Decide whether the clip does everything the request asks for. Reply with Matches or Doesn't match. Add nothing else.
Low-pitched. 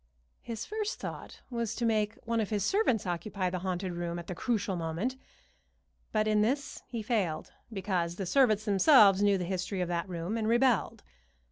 Doesn't match